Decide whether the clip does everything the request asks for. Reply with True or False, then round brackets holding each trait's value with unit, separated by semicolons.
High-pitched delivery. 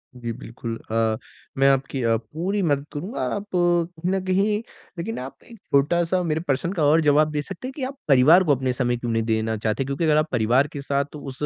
False (145 Hz)